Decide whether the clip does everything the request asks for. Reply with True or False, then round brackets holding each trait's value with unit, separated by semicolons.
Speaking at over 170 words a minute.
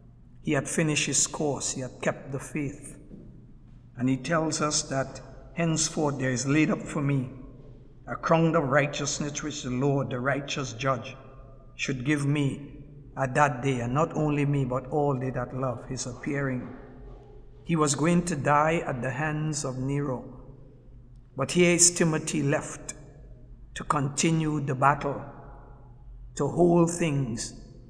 False (155 wpm)